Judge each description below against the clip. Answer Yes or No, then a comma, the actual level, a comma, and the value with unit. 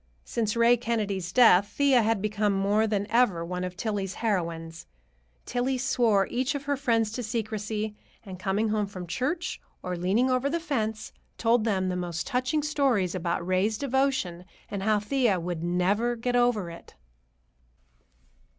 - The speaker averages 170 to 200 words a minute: No, average, 160 wpm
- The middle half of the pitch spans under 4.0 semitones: No, average, 4.6 semitones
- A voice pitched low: No, high, 215 Hz